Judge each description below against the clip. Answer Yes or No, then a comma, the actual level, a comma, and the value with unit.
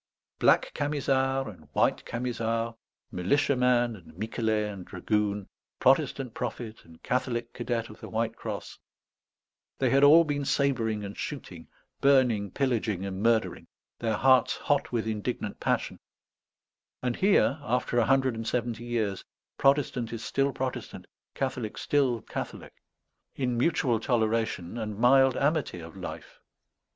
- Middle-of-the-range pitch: No, low, 120 Hz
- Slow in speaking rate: Yes, slow, 130 wpm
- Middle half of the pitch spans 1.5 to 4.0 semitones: Yes, average, 3.5 semitones